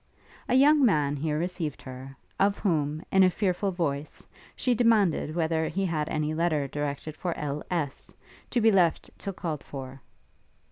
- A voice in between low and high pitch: Yes, medium, 160 Hz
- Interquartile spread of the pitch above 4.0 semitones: Yes, average, 4.5 semitones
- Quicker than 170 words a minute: No, average, 155 wpm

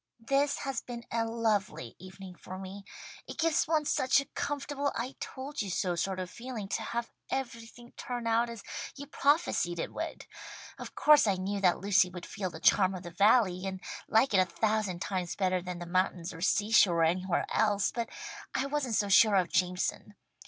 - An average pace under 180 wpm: No, average, 195 wpm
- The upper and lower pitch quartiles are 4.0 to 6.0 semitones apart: Yes, average, 4.7 semitones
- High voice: Yes, high, 205 Hz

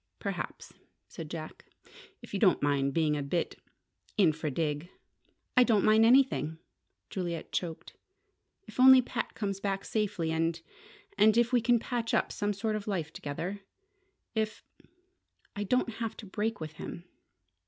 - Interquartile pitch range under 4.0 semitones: No, wide, 5.5 semitones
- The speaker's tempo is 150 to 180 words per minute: Yes, average, 155 wpm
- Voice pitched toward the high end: Yes, high, 200 Hz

